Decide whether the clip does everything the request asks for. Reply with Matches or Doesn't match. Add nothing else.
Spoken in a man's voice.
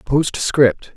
Matches